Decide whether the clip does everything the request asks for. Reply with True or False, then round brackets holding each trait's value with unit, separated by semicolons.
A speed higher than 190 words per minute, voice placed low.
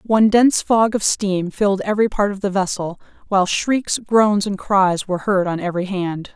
False (200 wpm; 200 Hz)